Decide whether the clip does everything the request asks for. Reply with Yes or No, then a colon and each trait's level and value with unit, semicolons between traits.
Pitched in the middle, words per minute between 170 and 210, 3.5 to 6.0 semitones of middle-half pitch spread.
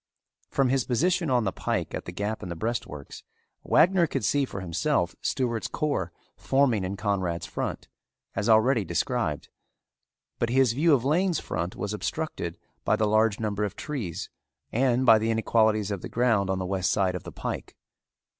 No: low, 110 Hz; average, 175 wpm; average, 5.2 semitones